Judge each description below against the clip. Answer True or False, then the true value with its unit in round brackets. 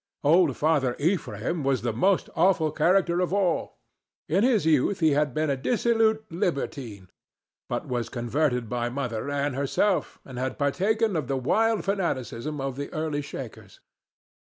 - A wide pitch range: True (5.9 semitones)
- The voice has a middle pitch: True (150 Hz)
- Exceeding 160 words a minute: False (155 wpm)